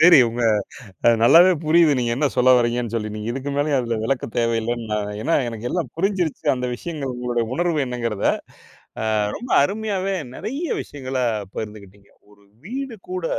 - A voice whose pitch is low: Yes, low, 130 Hz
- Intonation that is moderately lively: No, wide, 6.7 semitones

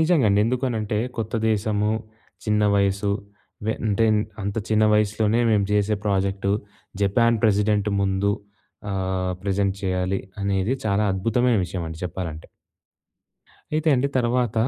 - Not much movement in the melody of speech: Yes, narrow, 2.3 semitones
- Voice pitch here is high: No, low, 105 Hz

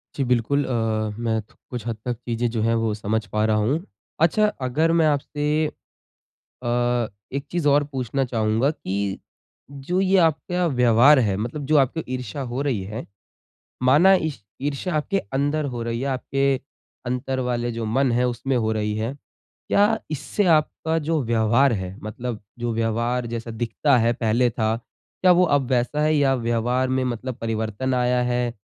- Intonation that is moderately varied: Yes, average, 3.7 semitones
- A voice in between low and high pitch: No, low, 125 Hz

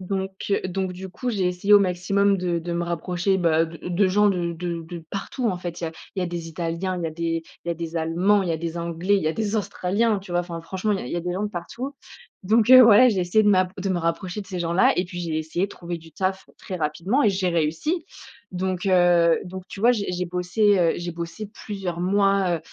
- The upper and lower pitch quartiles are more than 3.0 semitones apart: No, average, 2.7 semitones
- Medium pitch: Yes, medium, 180 Hz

